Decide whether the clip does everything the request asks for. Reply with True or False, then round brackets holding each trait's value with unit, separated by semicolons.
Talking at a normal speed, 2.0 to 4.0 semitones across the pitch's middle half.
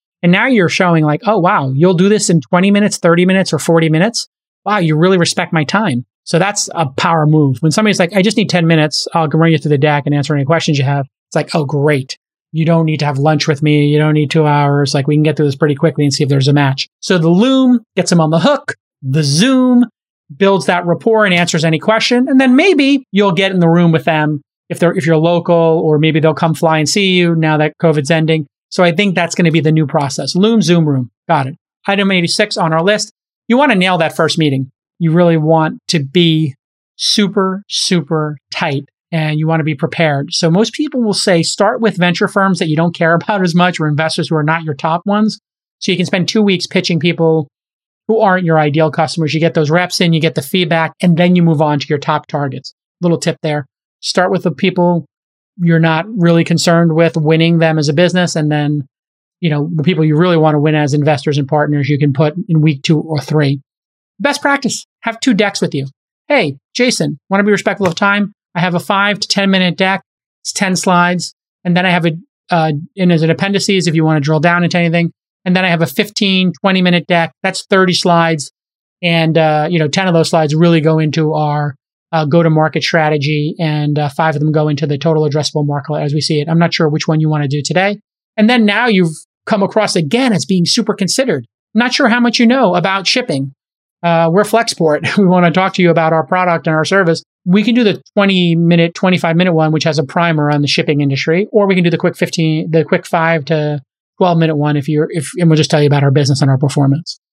False (245 wpm; 3.4 semitones)